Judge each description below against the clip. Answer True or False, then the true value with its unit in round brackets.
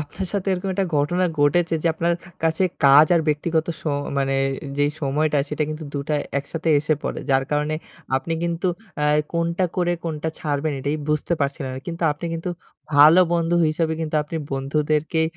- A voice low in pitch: False (155 Hz)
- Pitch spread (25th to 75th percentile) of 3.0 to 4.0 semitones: False (2.4 semitones)